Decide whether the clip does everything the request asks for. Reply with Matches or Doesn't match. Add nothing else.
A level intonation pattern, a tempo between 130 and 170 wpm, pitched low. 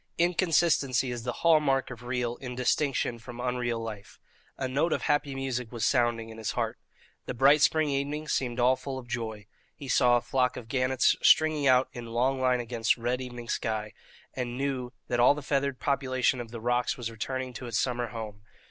Doesn't match